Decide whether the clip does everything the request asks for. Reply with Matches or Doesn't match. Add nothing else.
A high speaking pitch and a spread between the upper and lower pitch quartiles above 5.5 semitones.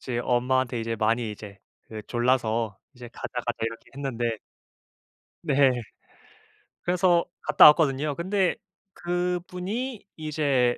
Doesn't match